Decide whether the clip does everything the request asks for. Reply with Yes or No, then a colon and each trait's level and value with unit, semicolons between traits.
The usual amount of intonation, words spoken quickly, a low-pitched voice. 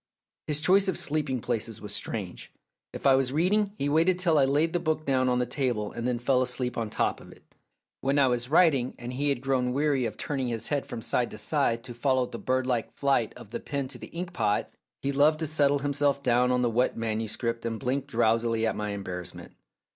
Yes: average, 3.5 semitones; fast, 225 wpm; low, 130 Hz